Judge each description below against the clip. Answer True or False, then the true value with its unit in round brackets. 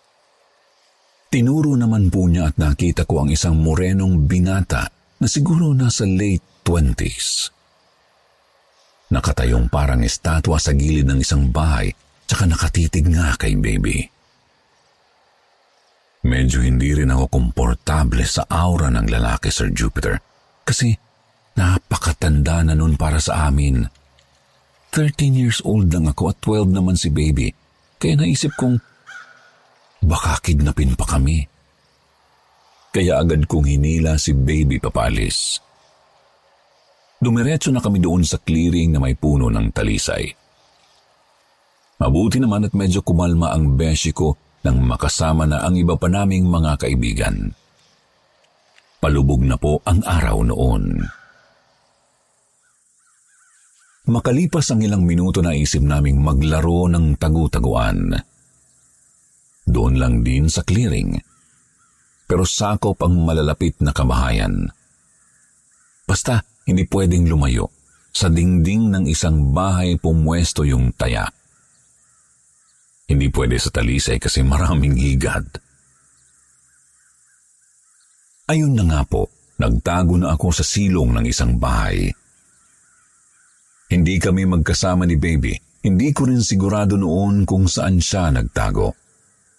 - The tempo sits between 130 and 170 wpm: False (115 wpm)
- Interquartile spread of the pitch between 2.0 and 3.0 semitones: False (4.4 semitones)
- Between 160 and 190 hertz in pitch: False (80 Hz)